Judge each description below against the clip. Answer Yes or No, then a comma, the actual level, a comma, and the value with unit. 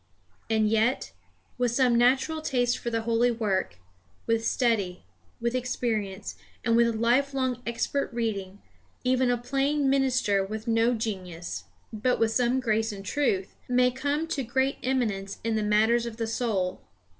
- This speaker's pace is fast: No, average, 155 wpm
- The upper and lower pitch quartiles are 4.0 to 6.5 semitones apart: No, average, 2.7 semitones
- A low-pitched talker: No, high, 235 Hz